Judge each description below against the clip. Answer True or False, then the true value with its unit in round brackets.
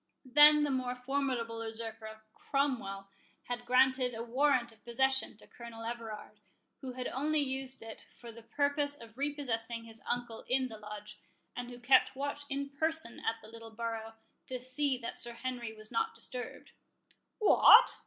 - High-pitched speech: True (245 Hz)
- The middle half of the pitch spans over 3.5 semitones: False (3.1 semitones)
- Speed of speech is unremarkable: True (165 wpm)